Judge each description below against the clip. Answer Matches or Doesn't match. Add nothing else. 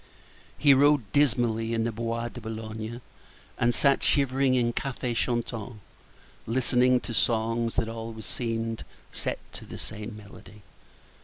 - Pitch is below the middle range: Matches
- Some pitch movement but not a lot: Doesn't match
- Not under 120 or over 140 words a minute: Matches